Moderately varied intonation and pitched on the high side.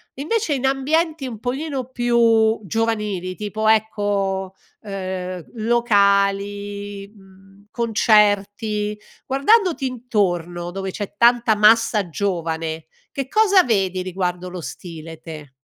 Yes: average, 4.0 semitones; high, 205 Hz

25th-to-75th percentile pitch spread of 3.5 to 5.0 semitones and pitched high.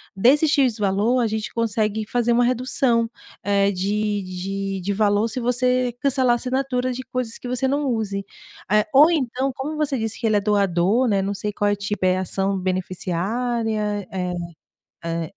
Yes: average, 4.0 semitones; high, 220 Hz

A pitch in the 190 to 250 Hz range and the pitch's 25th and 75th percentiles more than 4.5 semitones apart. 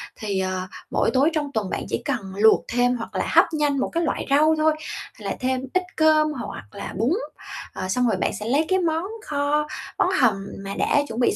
No: very high, 270 Hz; wide, 5.6 semitones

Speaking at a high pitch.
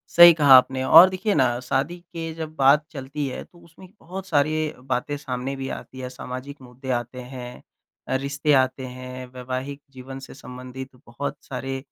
No: low, 135 Hz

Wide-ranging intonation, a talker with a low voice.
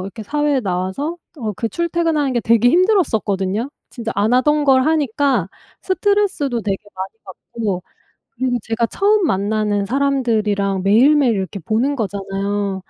No: wide, 6.2 semitones; high, 230 Hz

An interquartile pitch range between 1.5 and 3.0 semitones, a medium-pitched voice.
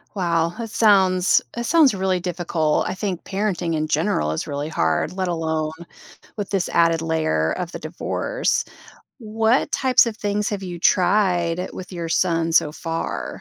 No: average, 3.7 semitones; medium, 180 Hz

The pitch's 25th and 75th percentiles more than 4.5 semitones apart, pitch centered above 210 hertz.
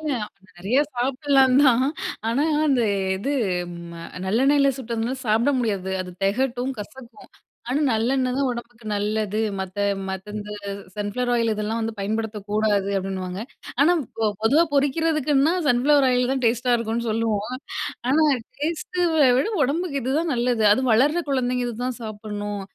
No: average, 4.0 semitones; high, 240 Hz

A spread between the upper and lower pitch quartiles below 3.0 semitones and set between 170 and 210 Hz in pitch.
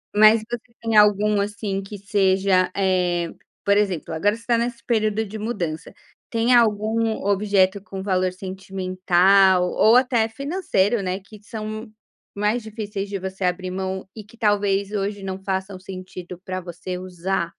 Yes: narrow, 2.4 semitones; high, 200 Hz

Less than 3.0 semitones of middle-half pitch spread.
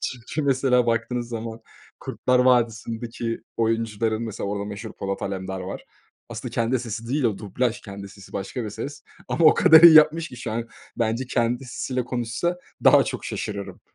Yes: narrow, 2.6 semitones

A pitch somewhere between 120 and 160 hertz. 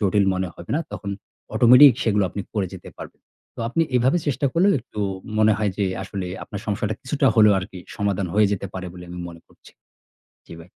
No: low, 105 Hz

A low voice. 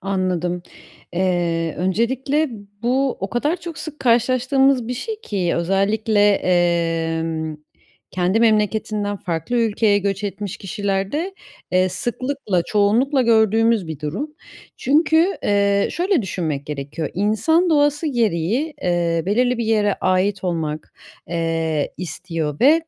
No: high, 205 Hz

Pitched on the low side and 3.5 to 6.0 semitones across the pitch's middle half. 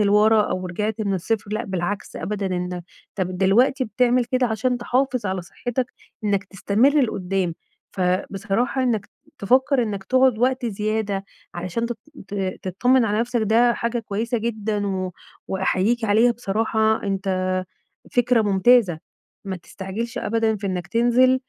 No: high, 215 Hz; average, 3.8 semitones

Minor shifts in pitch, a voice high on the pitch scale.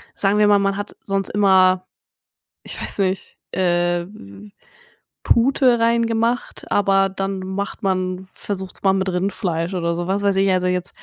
Yes: narrow, 1.8 semitones; high, 195 Hz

